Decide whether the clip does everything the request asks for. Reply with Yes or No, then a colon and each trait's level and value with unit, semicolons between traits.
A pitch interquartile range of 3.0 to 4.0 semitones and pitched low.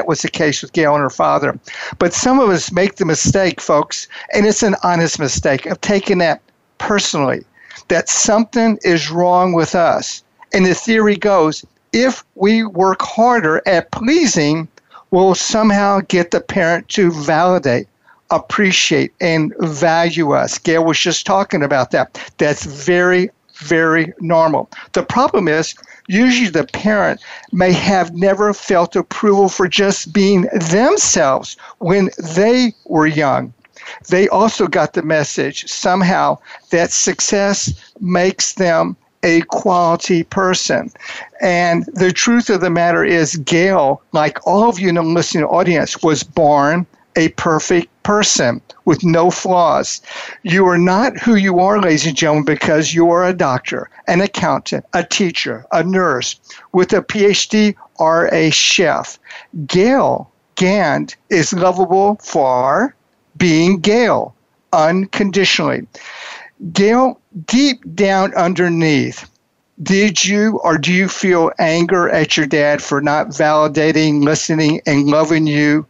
No: average, 3.6 semitones; medium, 180 Hz